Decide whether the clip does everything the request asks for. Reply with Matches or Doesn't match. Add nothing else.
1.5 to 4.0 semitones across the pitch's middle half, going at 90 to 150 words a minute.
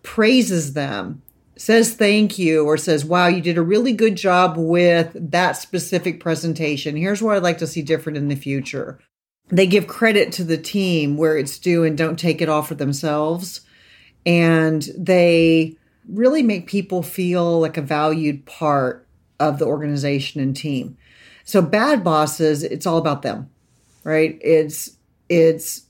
Doesn't match